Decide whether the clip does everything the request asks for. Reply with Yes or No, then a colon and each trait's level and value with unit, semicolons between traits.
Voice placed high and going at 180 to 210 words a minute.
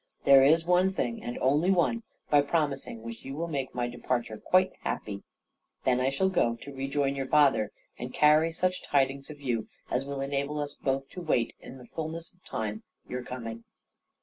No: medium, 140 Hz; average, 190 wpm